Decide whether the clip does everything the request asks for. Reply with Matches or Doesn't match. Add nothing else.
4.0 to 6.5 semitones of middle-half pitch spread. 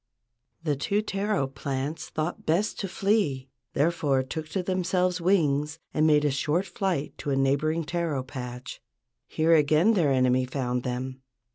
Matches